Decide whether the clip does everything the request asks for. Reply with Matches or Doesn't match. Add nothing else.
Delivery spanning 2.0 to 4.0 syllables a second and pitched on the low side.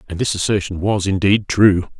Doesn't match